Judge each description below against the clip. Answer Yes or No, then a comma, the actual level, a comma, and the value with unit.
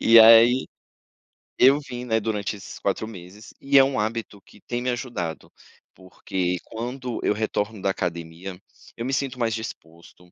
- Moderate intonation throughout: Yes, average, 4.4 semitones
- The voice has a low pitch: Yes, low, 110 Hz